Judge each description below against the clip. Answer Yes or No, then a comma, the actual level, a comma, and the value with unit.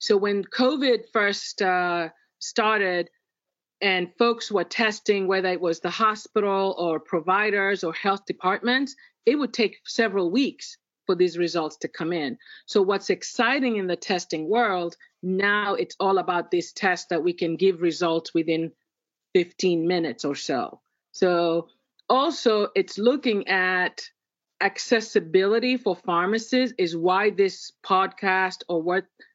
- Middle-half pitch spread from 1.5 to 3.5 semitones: No, average, 4.0 semitones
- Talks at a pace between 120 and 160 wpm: Yes, average, 140 wpm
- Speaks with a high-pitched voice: Yes, high, 195 Hz